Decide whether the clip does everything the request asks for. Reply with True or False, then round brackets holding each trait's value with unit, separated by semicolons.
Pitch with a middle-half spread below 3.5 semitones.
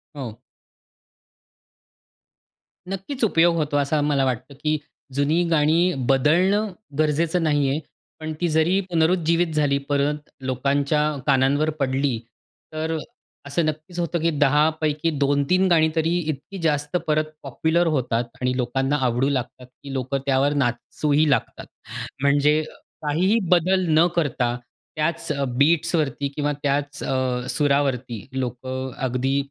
True (3.0 semitones)